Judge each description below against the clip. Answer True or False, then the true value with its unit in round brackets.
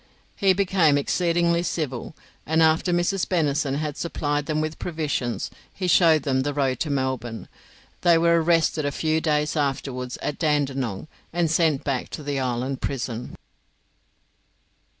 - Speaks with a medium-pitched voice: True (150 Hz)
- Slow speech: False (145 wpm)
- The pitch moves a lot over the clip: False (3.6 semitones)